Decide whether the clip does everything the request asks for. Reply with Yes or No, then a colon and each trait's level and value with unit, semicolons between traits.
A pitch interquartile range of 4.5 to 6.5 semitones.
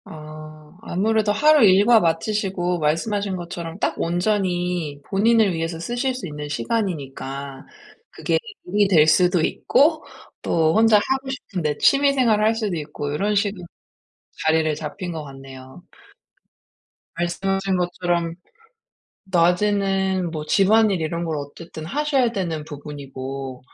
Yes: average, 5.1 semitones